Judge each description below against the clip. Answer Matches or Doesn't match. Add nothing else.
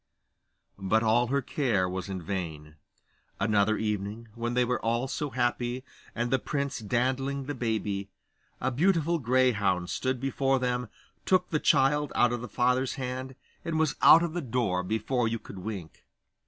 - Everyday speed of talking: Matches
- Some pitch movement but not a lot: Matches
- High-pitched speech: Doesn't match